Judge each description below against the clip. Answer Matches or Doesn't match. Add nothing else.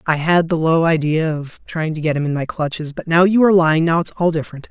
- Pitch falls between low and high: Matches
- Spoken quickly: Matches